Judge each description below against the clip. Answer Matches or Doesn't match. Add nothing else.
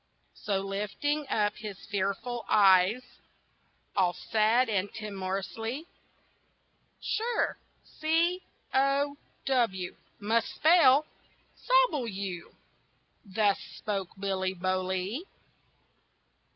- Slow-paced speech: Matches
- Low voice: Doesn't match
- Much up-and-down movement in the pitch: Matches